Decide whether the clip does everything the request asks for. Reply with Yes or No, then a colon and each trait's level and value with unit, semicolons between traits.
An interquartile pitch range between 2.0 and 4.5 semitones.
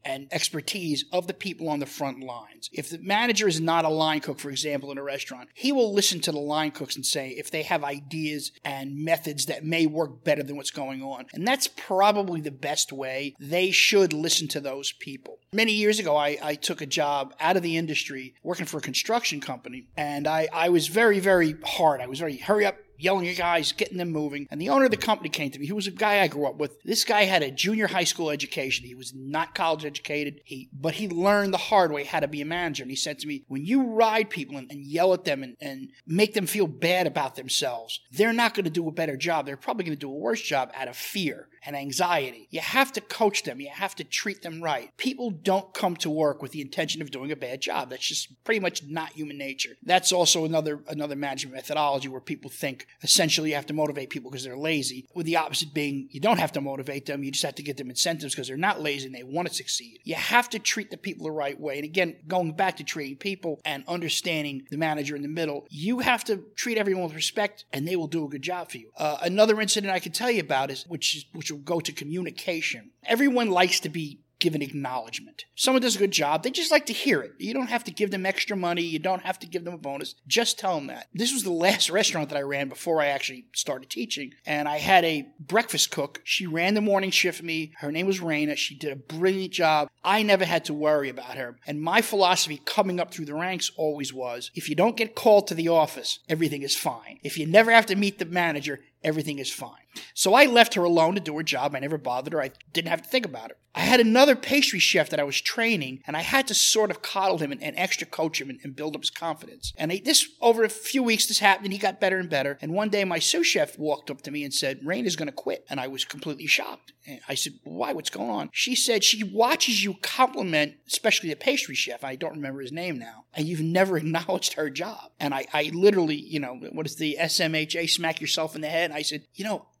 No: average, 5.0 semitones